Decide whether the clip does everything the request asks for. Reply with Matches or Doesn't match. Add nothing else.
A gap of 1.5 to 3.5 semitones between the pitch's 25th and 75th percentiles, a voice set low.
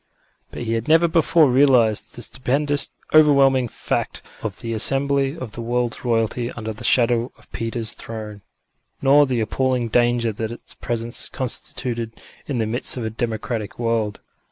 Matches